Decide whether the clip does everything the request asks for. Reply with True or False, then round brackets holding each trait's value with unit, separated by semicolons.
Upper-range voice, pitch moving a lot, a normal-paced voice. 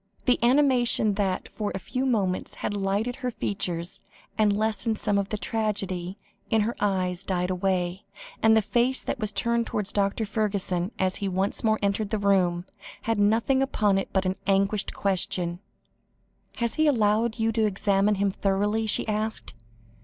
False (205 Hz; 2.4 semitones; 170 wpm)